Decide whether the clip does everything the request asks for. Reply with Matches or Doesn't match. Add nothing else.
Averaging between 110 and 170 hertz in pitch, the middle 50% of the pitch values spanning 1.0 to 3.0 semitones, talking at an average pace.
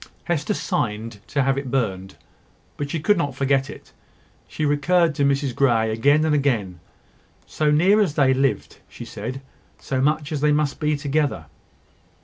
Matches